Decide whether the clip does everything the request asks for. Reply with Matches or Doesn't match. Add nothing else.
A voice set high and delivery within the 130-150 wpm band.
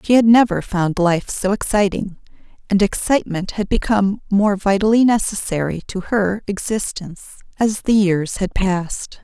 Matches